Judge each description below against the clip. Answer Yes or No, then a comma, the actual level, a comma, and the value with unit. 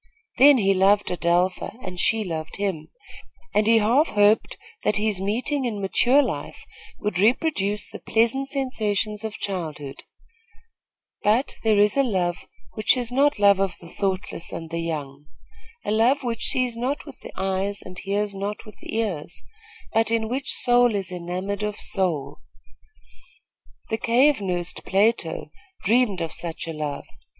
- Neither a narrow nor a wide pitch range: Yes, average, 4.1 semitones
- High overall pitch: Yes, high, 205 Hz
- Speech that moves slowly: No, average, 160 wpm